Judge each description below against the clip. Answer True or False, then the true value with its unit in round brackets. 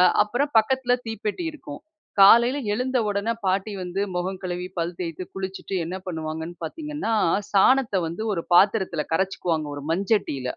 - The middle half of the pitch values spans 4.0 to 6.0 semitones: True (4.5 semitones)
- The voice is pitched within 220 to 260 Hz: False (190 Hz)